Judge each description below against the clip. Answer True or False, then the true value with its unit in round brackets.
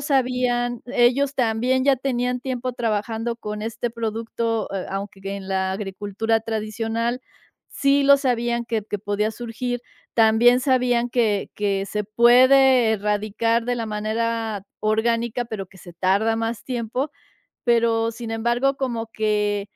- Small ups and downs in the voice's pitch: True (2.3 semitones)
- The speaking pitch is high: True (230 Hz)